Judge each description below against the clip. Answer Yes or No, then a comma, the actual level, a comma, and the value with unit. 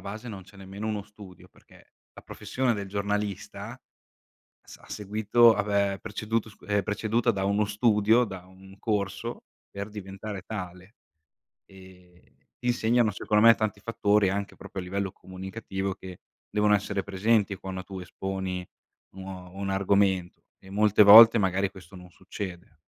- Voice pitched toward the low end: Yes, low, 100 Hz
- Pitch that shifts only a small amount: Yes, narrow, 1.9 semitones